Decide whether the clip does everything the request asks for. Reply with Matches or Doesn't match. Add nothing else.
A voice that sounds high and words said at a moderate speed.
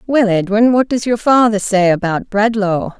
Matches